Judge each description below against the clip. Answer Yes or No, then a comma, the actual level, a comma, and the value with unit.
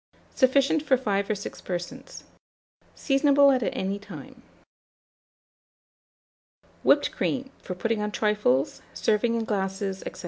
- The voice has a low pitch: No, high, 215 Hz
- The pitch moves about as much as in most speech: Yes, average, 5.0 semitones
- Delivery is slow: Yes, slow, 115 wpm